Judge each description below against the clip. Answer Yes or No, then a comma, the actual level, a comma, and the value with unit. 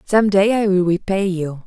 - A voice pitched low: No, high, 190 Hz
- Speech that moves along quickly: Yes, fast, 215 wpm